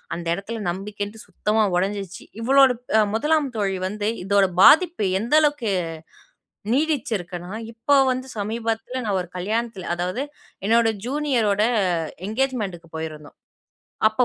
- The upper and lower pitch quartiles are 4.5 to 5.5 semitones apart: Yes, average, 4.8 semitones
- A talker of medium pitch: No, high, 215 Hz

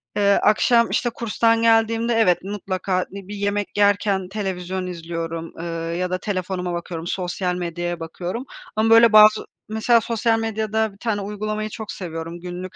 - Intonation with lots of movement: No, average, 3.6 semitones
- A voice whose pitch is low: No, high, 200 Hz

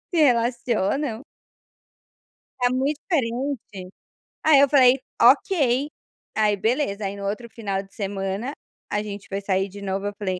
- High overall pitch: Yes, high, 220 Hz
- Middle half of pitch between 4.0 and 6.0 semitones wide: Yes, average, 4.8 semitones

